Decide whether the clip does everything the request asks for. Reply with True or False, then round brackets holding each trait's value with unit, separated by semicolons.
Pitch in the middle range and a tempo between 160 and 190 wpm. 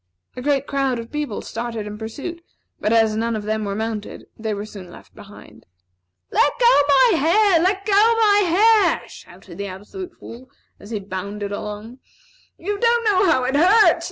False (250 Hz; 180 wpm)